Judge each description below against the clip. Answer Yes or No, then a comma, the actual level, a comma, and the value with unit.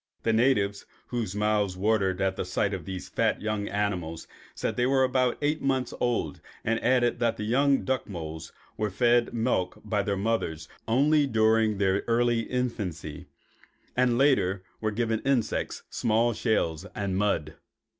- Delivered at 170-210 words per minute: No, average, 160 wpm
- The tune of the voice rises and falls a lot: No, average, 3.9 semitones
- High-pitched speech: No, low, 110 Hz